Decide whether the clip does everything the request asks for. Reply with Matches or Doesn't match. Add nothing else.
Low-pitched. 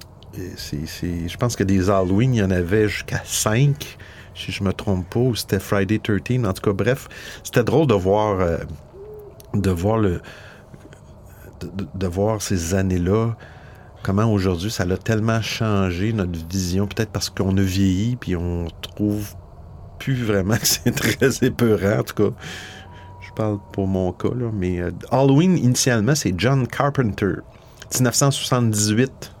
Matches